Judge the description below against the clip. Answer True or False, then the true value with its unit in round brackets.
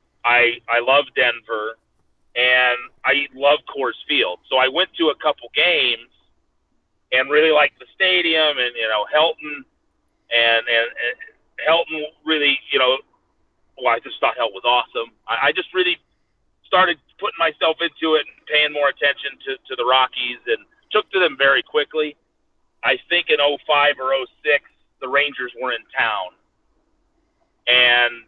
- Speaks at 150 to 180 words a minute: True (155 wpm)